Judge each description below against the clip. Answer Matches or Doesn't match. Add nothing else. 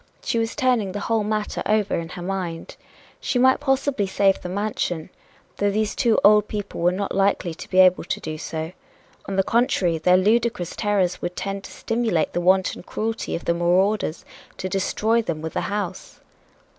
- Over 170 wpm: Matches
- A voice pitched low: Doesn't match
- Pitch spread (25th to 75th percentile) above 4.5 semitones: Doesn't match